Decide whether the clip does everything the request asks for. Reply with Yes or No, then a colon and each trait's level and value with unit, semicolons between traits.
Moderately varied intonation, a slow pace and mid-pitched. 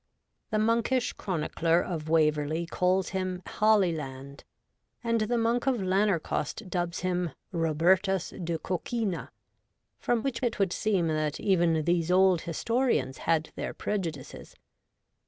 Yes: average, 4.6 semitones; slow, 125 wpm; medium, 180 Hz